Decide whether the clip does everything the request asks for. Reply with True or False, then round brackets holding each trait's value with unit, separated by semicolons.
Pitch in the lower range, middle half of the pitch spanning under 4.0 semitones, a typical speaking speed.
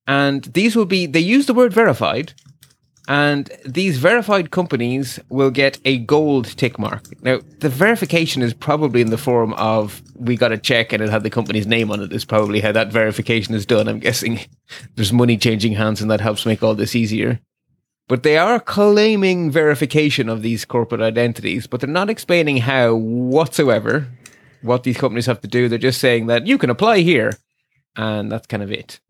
False (125 Hz; 4.4 semitones; 195 wpm)